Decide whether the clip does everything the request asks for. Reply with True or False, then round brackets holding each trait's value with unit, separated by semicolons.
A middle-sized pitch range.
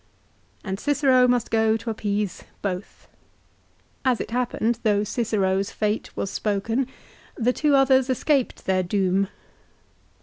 True (3.9 semitones)